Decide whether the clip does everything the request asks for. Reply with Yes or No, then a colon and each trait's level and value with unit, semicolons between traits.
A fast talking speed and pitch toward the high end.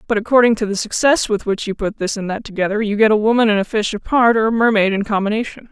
Yes: fast, 275 wpm; high, 215 Hz